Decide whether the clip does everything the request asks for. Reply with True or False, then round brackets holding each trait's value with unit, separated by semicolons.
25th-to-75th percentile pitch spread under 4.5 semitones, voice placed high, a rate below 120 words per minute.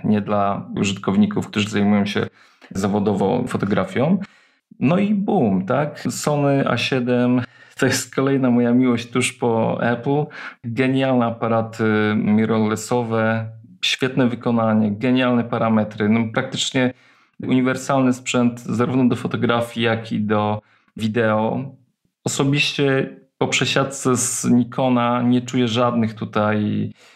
False (2.9 semitones; 120 Hz; 110 wpm)